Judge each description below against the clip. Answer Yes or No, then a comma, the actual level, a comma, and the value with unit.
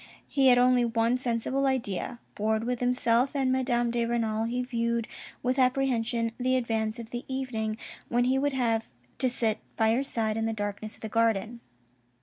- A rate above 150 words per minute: Yes, average, 180 wpm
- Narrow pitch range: Yes, narrow, 2.1 semitones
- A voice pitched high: Yes, high, 235 Hz